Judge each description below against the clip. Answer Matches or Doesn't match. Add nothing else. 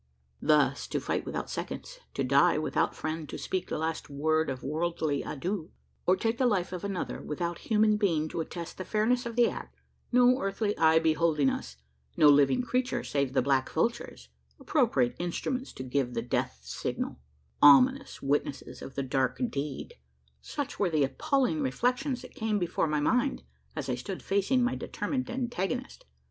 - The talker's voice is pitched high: Doesn't match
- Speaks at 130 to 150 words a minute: Doesn't match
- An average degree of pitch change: Doesn't match